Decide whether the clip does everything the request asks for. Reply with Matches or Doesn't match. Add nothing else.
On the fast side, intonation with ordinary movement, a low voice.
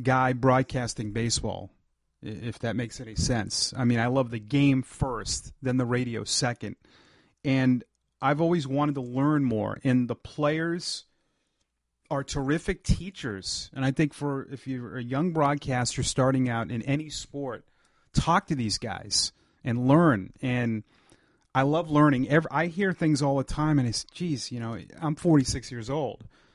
Doesn't match